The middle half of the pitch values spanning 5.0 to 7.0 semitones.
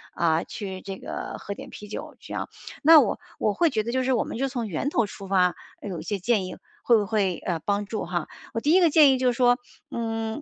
No: average, 4.6 semitones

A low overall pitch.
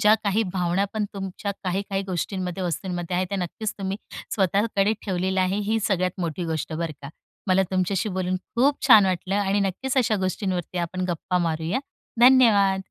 No: high, 190 Hz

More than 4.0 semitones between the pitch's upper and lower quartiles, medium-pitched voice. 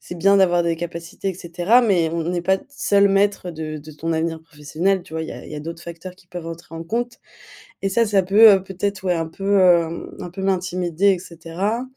No: average, 2.8 semitones; medium, 175 Hz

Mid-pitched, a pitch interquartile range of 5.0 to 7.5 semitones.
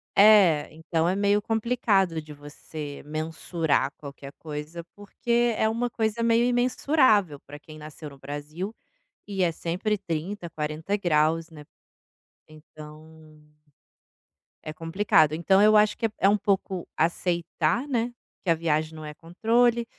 Yes: medium, 170 Hz; average, 5.3 semitones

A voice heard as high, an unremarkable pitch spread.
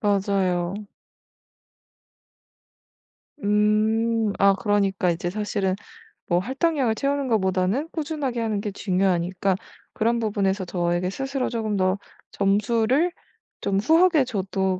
Yes: high, 205 Hz; average, 3.5 semitones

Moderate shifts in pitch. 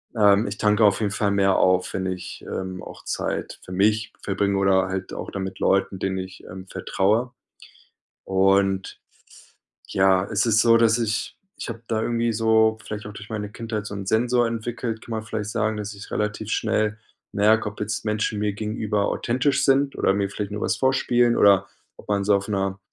No: narrow, 2.3 semitones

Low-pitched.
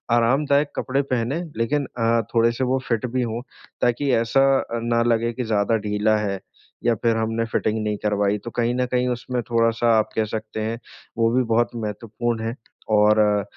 Yes: low, 115 Hz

